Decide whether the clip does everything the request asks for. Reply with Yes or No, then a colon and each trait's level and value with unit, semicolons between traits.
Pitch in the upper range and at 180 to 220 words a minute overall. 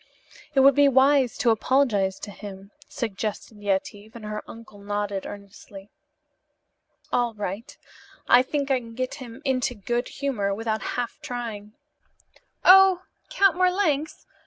No: high, 230 Hz; slow, 135 wpm